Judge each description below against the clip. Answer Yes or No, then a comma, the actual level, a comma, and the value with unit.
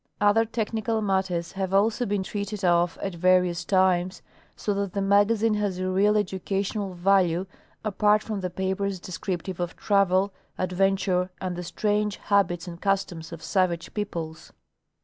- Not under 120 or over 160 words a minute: Yes, average, 150 wpm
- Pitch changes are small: Yes, narrow, 2.3 semitones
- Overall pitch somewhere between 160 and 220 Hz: Yes, high, 190 Hz